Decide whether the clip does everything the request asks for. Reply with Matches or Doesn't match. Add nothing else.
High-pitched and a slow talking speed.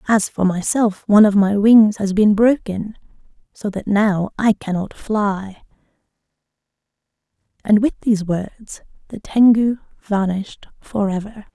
Matches